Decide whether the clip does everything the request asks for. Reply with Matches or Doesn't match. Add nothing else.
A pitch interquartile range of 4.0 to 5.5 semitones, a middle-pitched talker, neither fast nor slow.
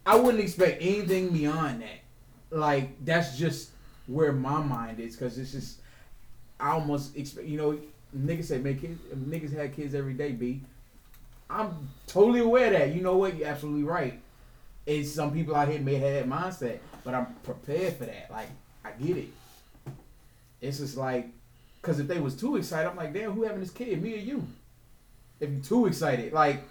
Matches